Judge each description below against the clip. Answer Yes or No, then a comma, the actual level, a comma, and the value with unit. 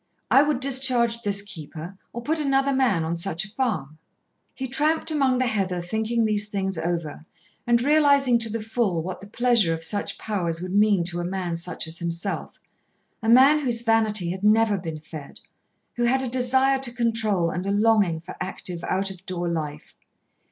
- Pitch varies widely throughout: Yes, wide, 5.8 semitones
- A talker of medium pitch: No, high, 210 Hz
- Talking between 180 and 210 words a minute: Yes, average, 185 wpm